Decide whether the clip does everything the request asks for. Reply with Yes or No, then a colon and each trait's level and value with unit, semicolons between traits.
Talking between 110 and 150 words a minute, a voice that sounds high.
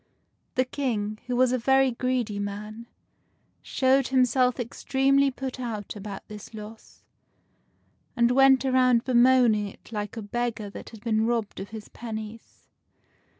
Yes: average, 140 wpm; high, 235 Hz